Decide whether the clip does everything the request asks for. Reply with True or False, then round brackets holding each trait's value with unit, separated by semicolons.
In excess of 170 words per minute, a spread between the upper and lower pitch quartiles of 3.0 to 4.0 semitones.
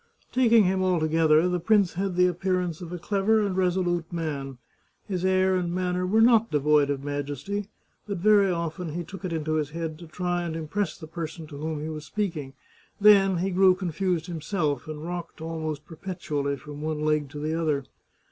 True (190 wpm; 3.4 semitones)